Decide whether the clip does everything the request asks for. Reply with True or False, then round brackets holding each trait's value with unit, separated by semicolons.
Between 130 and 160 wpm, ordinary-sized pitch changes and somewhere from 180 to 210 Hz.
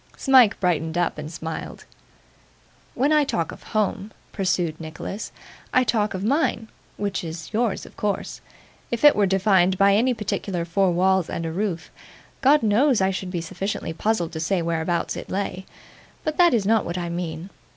False (175 wpm; 4.2 semitones; 190 Hz)